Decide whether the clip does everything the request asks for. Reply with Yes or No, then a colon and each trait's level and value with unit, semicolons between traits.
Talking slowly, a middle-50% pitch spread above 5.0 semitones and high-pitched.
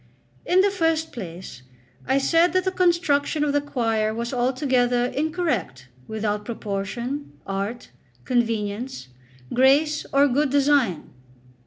Yes: slow, 120 wpm; wide, 5.4 semitones; very high, 255 Hz